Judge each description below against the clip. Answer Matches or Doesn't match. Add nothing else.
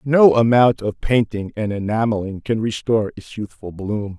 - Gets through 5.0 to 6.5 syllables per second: Doesn't match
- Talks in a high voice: Doesn't match